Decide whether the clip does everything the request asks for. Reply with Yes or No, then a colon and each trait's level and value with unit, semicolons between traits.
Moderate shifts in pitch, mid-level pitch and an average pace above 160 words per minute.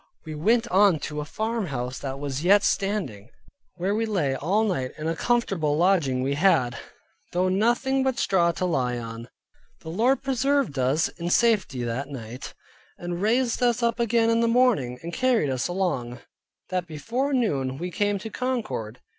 No: wide, 8.9 semitones; medium, 180 Hz; average, 170 wpm